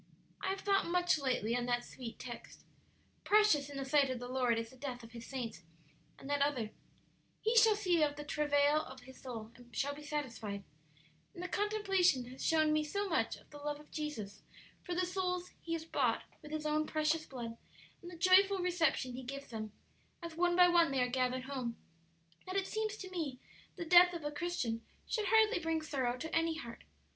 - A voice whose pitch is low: No, very high, 300 Hz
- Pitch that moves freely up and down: Yes, wide, 5.7 semitones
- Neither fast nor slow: No, fast, 210 wpm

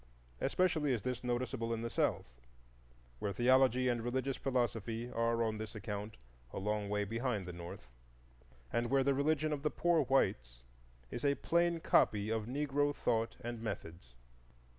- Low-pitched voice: Yes, low, 120 Hz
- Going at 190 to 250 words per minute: No, average, 160 wpm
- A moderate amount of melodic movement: Yes, average, 4.1 semitones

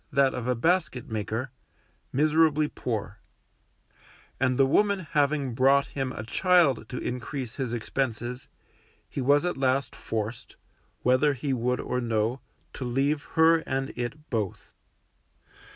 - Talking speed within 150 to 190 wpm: No, slow, 135 wpm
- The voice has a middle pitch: No, low, 130 Hz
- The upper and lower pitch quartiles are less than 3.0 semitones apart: No, average, 3.3 semitones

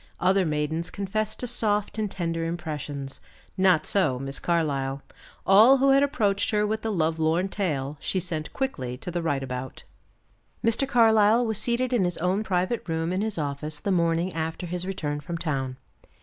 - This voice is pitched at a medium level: Yes, medium, 175 Hz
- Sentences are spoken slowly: No, average, 175 wpm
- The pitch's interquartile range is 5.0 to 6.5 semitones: Yes, average, 5.3 semitones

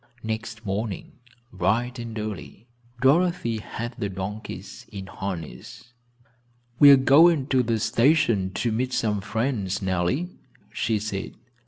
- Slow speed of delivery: Yes, slow, 125 wpm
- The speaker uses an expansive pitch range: No, average, 4.3 semitones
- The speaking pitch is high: No, low, 110 Hz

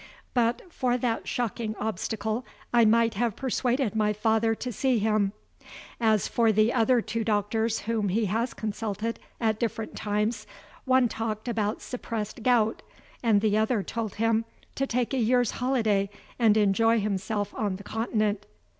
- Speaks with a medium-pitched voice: No, high, 220 Hz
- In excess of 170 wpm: No, average, 155 wpm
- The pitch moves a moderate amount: No, narrow, 1.8 semitones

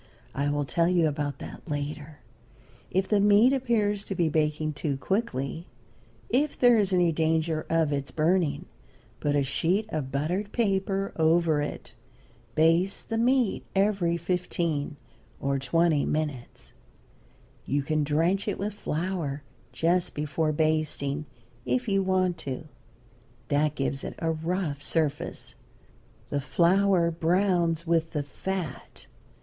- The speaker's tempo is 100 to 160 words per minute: Yes, slow, 135 wpm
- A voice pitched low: No, medium, 165 Hz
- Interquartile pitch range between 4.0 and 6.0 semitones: Yes, average, 4.3 semitones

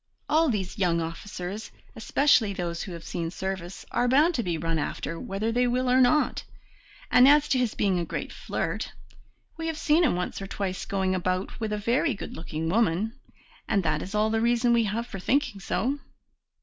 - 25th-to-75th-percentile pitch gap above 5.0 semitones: Yes, wide, 5.4 semitones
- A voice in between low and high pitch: No, high, 210 Hz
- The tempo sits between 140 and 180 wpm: No, average, 200 wpm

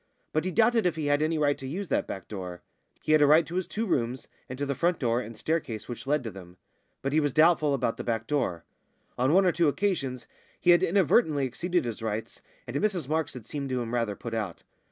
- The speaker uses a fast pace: Yes, fast, 245 wpm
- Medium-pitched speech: Yes, medium, 145 Hz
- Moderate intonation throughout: No, wide, 6.1 semitones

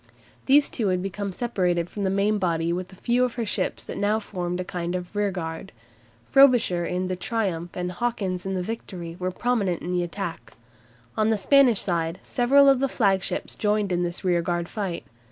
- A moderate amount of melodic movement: Yes, average, 3.7 semitones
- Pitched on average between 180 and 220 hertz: Yes, high, 190 Hz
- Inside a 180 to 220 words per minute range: Yes, average, 190 wpm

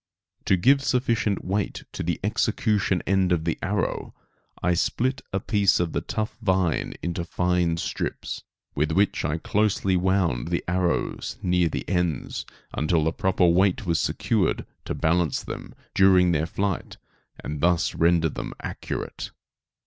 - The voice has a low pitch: Yes, very low, 90 Hz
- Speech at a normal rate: Yes, average, 150 wpm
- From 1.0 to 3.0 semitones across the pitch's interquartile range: Yes, average, 2.7 semitones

